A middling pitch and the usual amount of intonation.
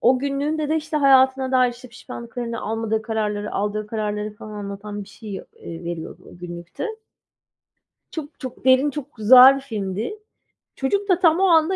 No: high, 245 Hz; average, 5.0 semitones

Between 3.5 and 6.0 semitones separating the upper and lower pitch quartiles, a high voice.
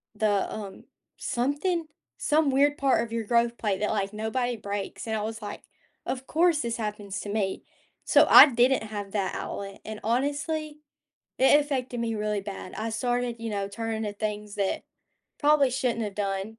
Yes: average, 4.0 semitones; high, 225 Hz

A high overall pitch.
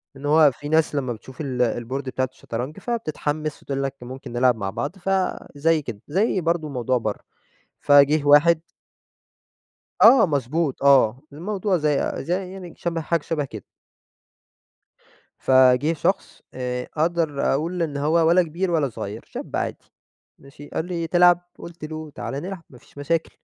No: medium, 150 Hz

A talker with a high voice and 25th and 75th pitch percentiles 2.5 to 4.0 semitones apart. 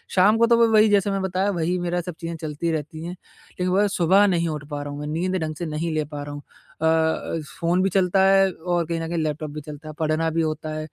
No: medium, 165 Hz; average, 2.9 semitones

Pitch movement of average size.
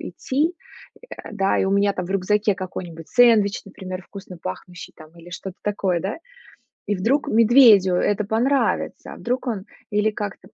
Yes: average, 3.1 semitones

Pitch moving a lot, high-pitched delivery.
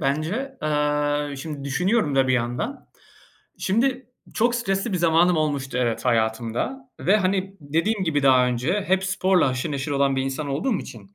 No: wide, 6.2 semitones; medium, 155 Hz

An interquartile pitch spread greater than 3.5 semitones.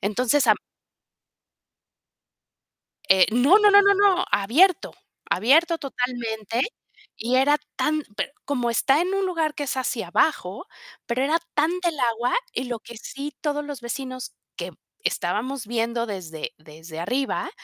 Yes: average, 5.2 semitones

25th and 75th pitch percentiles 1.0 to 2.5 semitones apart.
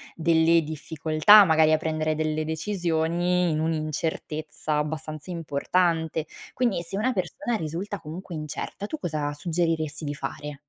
Yes: narrow, 2.0 semitones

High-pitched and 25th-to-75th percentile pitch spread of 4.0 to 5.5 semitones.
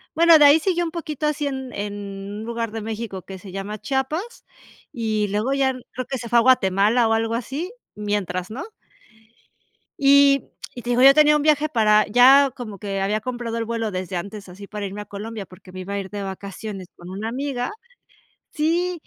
Yes: high, 230 Hz; average, 5.2 semitones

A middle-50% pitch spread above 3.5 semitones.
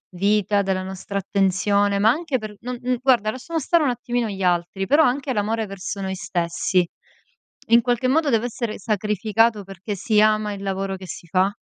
Yes: average, 3.9 semitones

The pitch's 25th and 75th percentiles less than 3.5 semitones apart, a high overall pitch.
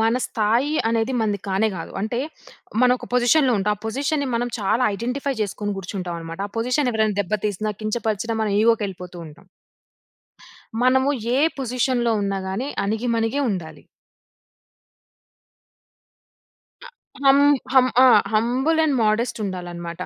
No: average, 3.9 semitones; high, 225 Hz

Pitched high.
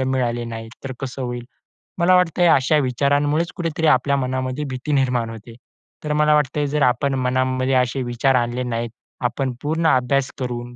No: low, 130 Hz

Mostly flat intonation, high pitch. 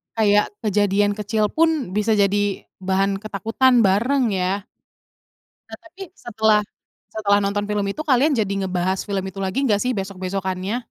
Yes: narrow, 2.3 semitones; high, 205 Hz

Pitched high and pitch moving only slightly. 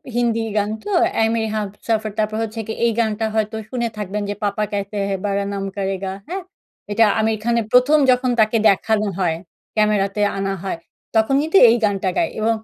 Yes: high, 215 Hz; narrow, 2.2 semitones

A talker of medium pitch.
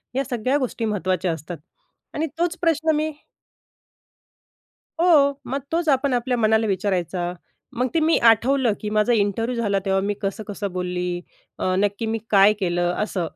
No: high, 215 Hz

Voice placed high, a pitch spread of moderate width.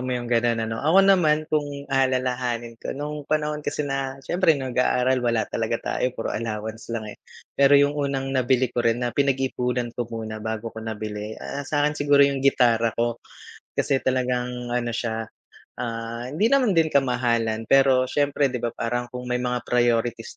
No: low, 125 Hz; average, 3.2 semitones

